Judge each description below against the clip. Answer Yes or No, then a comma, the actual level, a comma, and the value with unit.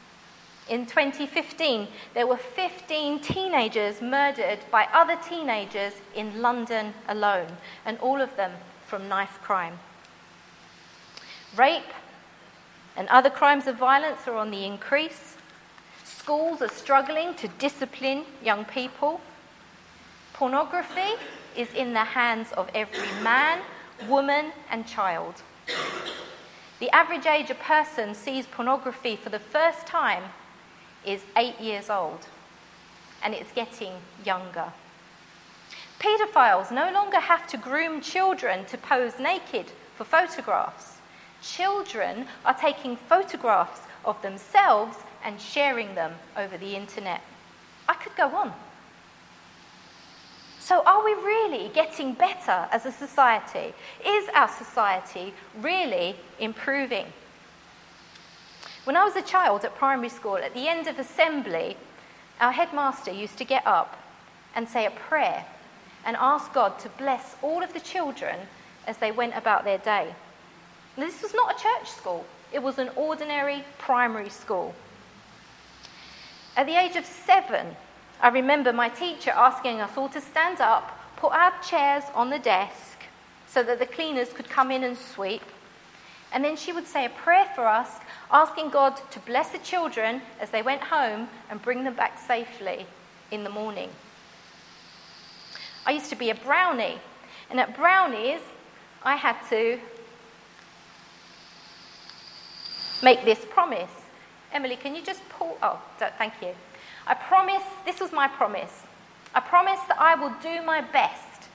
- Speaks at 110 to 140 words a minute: Yes, slow, 135 wpm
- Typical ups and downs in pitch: No, wide, 6.1 semitones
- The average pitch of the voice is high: Yes, very high, 270 Hz